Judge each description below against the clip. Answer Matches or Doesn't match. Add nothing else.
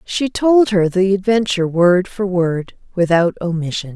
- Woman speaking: Matches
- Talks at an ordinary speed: Matches